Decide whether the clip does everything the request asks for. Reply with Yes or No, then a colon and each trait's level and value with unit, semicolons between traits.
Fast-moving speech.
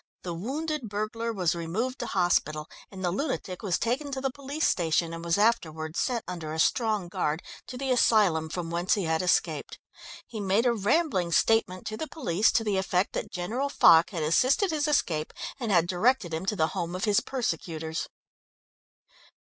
No: average, 185 wpm